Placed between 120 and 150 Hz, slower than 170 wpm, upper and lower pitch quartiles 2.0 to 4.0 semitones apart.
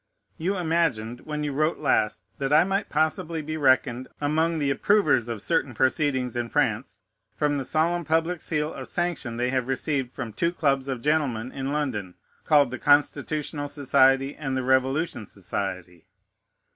Yes: medium, 140 Hz; average, 160 wpm; average, 3.7 semitones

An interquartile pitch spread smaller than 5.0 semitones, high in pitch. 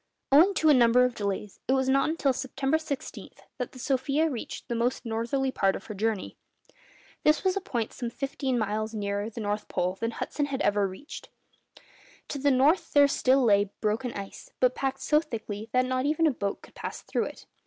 Yes: average, 4.4 semitones; very high, 255 Hz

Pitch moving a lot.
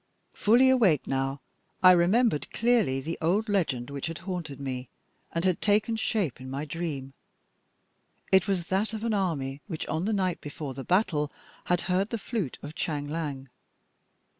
Yes: wide, 6.0 semitones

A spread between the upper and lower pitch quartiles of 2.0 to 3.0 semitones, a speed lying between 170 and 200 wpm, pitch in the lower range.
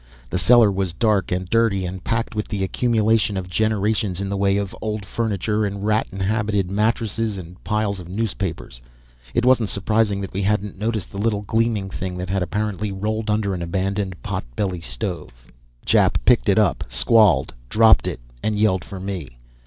Yes: narrow, 2.6 semitones; average, 175 wpm; low, 100 Hz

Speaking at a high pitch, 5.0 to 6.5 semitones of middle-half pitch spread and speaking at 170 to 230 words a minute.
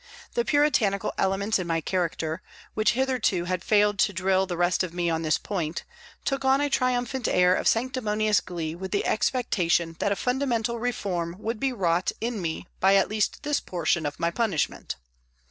Yes: high, 200 Hz; wide, 5.4 semitones; average, 180 wpm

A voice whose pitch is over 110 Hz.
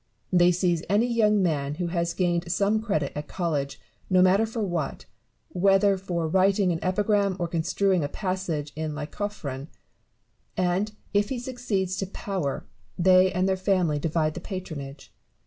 Yes: medium, 185 Hz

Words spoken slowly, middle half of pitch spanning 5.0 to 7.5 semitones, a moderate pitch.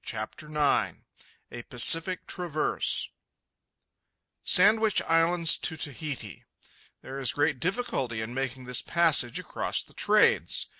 Yes: slow, 105 wpm; average, 5.3 semitones; medium, 150 Hz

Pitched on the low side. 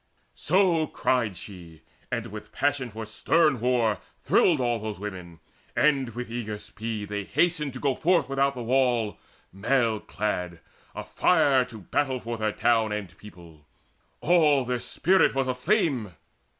Yes: low, 120 Hz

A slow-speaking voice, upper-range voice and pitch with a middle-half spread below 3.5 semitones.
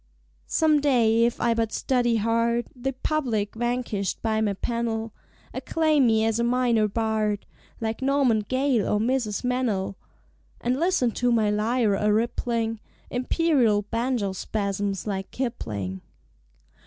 Yes: slow, 130 wpm; high, 230 Hz; average, 2.9 semitones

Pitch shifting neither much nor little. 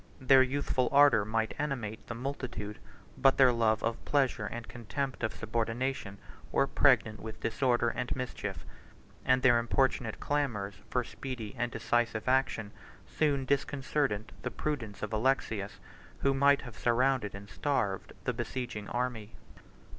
Yes: average, 3.3 semitones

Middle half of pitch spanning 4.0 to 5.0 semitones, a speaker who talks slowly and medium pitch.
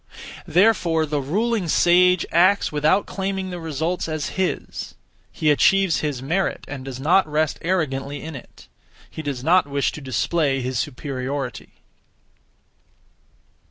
Yes: average, 4.5 semitones; slow, 130 wpm; medium, 155 Hz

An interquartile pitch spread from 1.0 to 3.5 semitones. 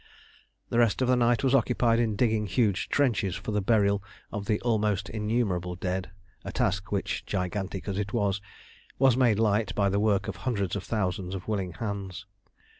Yes: average, 2.9 semitones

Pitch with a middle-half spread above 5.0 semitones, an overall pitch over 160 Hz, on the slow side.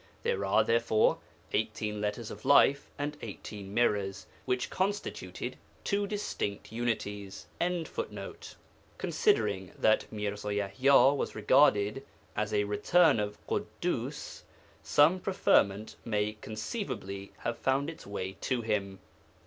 No: wide, 5.4 semitones; low, 110 Hz; slow, 110 wpm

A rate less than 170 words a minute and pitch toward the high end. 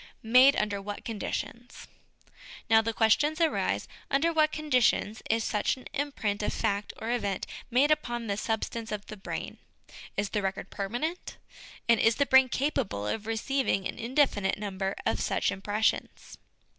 Yes: average, 155 wpm; high, 225 Hz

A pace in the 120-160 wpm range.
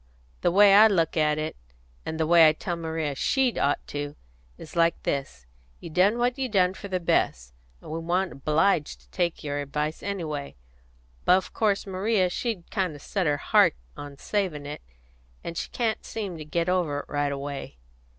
No: average, 190 wpm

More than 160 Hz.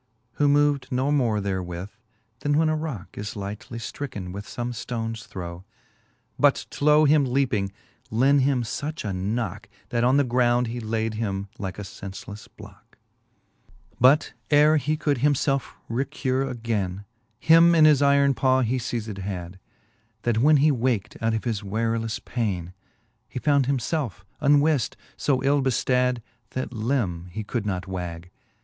No: low, 120 Hz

